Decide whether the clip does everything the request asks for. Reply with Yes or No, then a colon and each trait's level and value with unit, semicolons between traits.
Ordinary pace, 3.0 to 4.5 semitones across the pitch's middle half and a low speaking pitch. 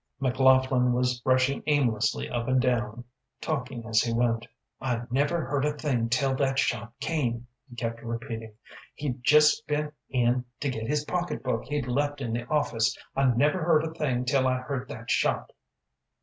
Yes: average, 170 wpm; average, 3.3 semitones; low, 130 Hz